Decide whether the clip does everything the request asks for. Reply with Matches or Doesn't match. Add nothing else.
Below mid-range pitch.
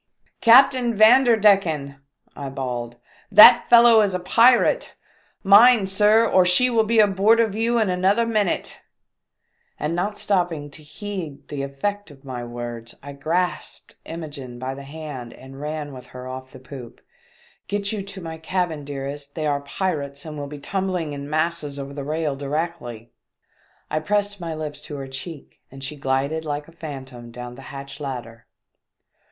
Doesn't match